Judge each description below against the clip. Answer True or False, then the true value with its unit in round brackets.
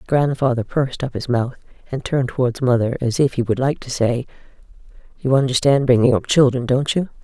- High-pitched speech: False (130 Hz)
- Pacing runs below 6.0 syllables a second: True (5.8 syllables/s)